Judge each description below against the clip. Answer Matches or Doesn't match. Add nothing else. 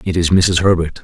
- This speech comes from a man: Matches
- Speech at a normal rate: Doesn't match